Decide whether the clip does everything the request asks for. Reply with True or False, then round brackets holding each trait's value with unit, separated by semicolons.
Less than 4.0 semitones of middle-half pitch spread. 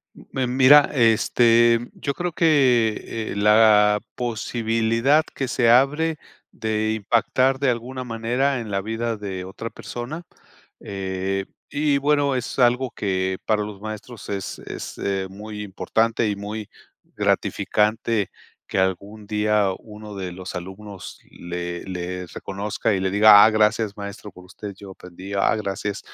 True (3.3 semitones)